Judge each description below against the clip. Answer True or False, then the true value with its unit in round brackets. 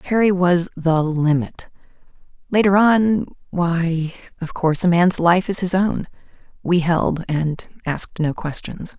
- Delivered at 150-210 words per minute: False (140 wpm)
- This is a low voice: False (175 Hz)